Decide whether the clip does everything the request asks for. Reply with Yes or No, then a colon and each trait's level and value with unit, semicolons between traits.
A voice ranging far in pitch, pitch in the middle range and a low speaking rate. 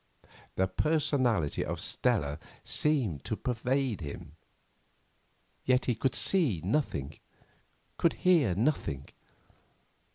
No: wide, 8.7 semitones; low, 120 Hz; slow, 95 wpm